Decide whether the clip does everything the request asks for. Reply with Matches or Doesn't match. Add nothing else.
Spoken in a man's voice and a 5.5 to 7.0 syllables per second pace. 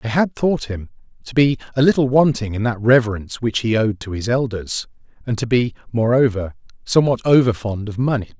Matches